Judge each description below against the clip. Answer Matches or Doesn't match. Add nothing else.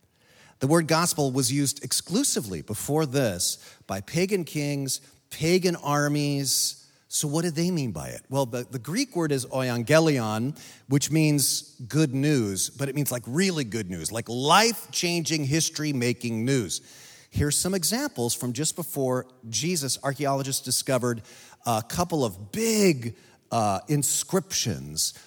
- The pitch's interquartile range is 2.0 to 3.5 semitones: Doesn't match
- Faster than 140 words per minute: Doesn't match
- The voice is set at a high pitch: Doesn't match